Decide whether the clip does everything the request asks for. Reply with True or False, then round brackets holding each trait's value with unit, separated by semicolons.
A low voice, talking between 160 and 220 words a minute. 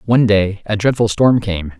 True (105 Hz; 200 wpm)